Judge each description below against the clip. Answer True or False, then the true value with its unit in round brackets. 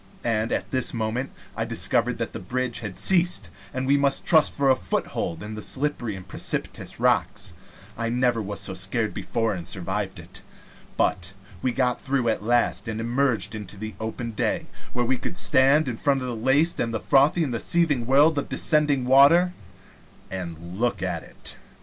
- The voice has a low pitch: True (120 Hz)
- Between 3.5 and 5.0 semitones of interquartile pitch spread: True (4.2 semitones)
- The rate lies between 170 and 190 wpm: True (180 wpm)